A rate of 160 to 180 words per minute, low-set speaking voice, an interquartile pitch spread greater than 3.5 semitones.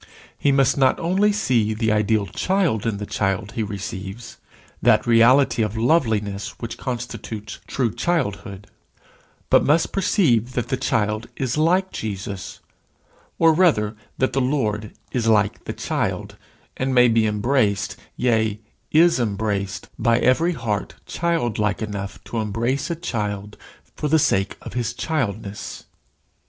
No: average, 140 wpm; low, 115 Hz; average, 4.6 semitones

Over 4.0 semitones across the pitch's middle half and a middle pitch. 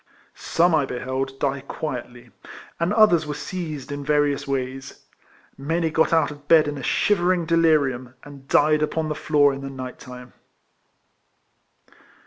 No: average, 3.0 semitones; medium, 145 Hz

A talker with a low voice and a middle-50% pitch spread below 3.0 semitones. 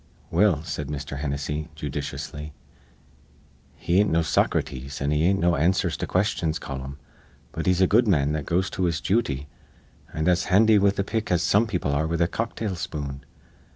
No: very low, 85 Hz; average, 4.5 semitones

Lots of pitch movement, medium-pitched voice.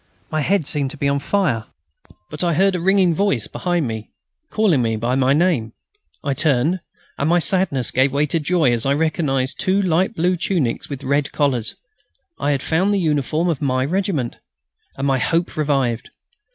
No: average, 4.7 semitones; medium, 150 Hz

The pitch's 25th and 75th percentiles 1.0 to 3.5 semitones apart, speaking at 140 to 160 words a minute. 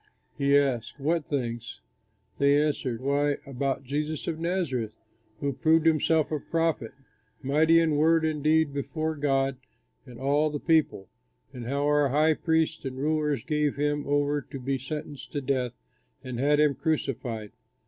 Yes: narrow, 2.5 semitones; average, 155 wpm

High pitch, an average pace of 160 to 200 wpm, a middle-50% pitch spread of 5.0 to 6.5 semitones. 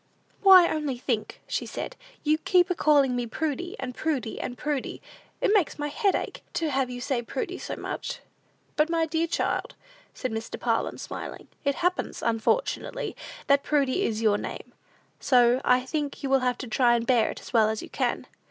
No: very high, 275 Hz; average, 190 wpm; average, 4.6 semitones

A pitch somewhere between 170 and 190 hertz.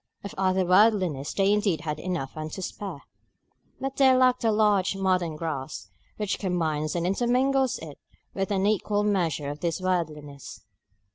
Yes: medium, 185 Hz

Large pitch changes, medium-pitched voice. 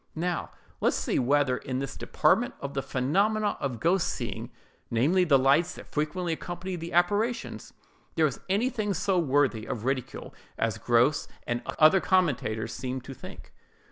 Yes: wide, 6.1 semitones; medium, 150 Hz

